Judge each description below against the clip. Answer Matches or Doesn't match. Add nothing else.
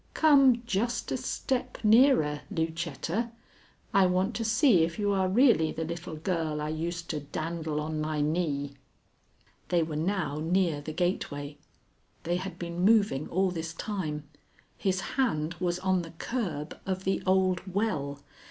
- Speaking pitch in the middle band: Matches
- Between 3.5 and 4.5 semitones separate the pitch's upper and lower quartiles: Matches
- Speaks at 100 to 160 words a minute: Matches